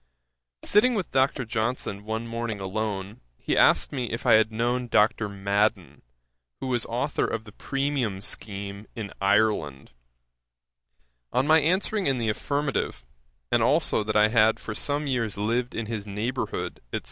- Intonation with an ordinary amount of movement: Yes, average, 3.5 semitones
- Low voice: Yes, low, 115 Hz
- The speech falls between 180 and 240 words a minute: No, average, 155 wpm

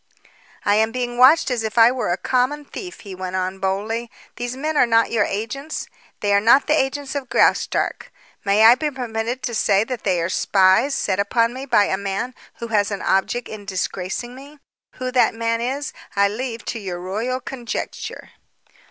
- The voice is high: Yes, high, 230 Hz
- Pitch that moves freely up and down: No, average, 4.2 semitones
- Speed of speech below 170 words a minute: No, average, 195 wpm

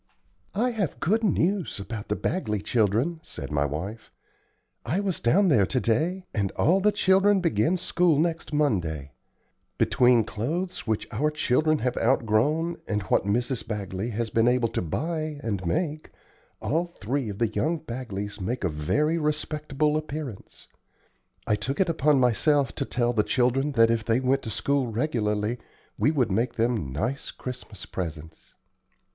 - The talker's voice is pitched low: Yes, low, 125 Hz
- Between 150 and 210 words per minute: Yes, average, 160 wpm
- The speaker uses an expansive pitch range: Yes, wide, 6.6 semitones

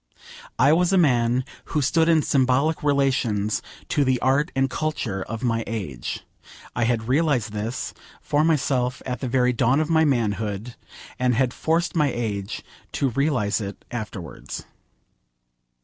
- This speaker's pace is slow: No, average, 150 wpm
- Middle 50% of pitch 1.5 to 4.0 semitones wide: No, average, 4.4 semitones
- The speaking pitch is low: Yes, low, 125 Hz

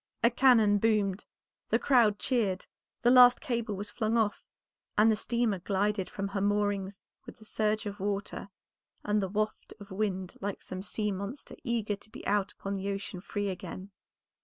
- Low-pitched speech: No, high, 205 Hz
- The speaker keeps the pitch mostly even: Yes, narrow, 1.8 semitones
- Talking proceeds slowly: No, average, 175 wpm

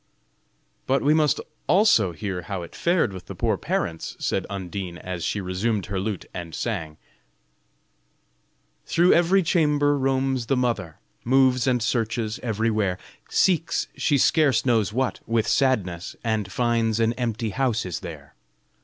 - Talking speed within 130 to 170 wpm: Yes, average, 145 wpm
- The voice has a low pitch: Yes, low, 115 Hz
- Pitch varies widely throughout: Yes, wide, 5.8 semitones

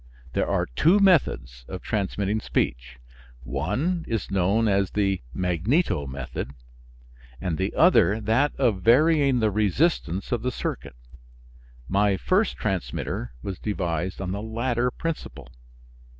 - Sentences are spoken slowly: Yes, slow, 125 wpm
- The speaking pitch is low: Yes, low, 100 Hz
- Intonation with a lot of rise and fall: Yes, wide, 5.8 semitones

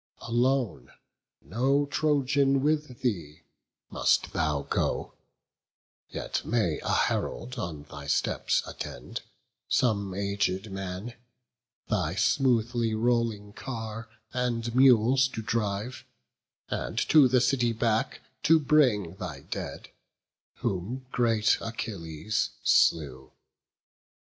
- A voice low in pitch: Yes, low, 115 Hz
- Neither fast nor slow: No, slow, 100 wpm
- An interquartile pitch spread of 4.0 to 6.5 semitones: Yes, average, 4.7 semitones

